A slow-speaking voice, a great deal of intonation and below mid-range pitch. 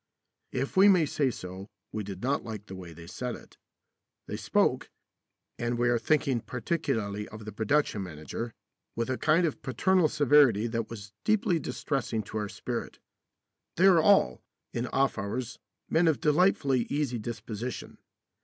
No: average, 160 wpm; wide, 5.9 semitones; low, 120 Hz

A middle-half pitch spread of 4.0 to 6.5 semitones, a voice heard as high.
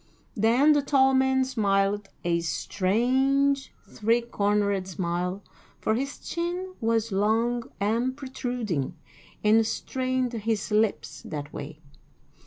Yes: average, 4.6 semitones; high, 225 Hz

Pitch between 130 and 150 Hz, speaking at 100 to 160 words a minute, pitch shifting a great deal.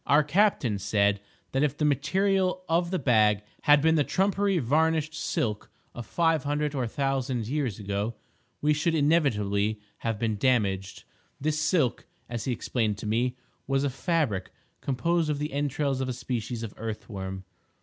No: low, 135 Hz; average, 170 wpm; wide, 5.8 semitones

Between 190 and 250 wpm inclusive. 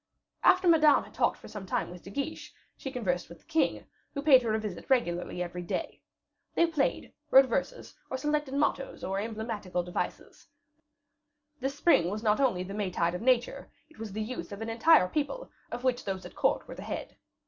Yes: average, 200 wpm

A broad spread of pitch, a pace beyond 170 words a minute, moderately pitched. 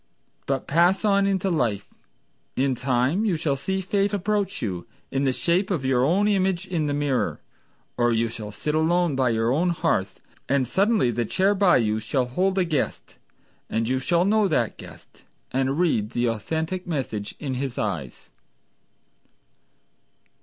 No: wide, 7.3 semitones; average, 165 wpm; medium, 145 Hz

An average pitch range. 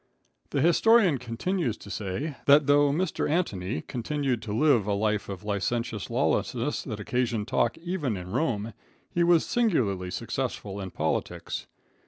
No: wide, 7.0 semitones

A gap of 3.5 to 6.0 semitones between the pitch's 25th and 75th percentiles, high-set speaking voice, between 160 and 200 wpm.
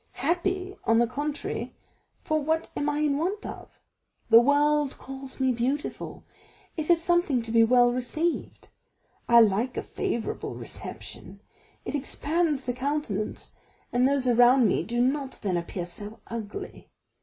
No: average, 4.1 semitones; very high, 265 Hz; average, 145 wpm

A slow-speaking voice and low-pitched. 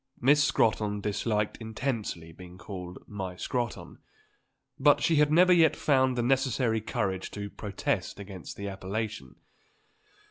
Yes: slow, 130 wpm; low, 110 Hz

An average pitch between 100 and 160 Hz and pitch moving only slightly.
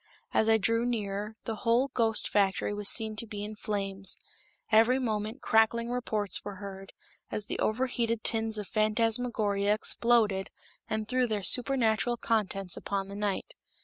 No: high, 215 Hz; narrow, 2.2 semitones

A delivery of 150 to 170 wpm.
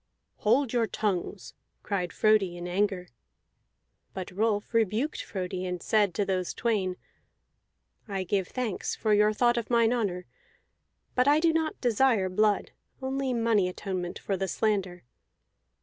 No: average, 140 wpm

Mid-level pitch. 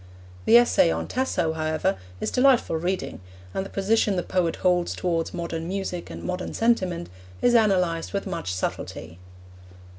Yes: medium, 180 Hz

